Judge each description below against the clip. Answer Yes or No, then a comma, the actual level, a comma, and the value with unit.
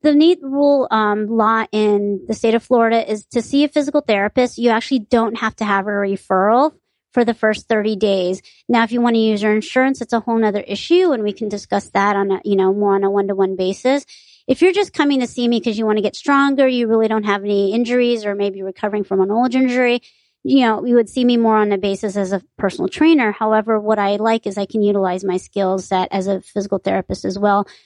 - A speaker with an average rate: No, fast, 245 wpm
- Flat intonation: No, average, 3.3 semitones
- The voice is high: Yes, high, 220 Hz